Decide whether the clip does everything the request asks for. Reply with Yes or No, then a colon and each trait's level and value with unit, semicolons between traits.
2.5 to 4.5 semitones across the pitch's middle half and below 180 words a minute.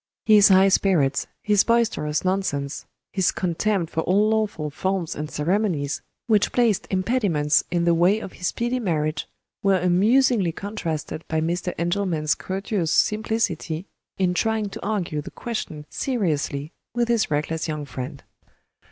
No: average, 5.2 semitones; average, 140 wpm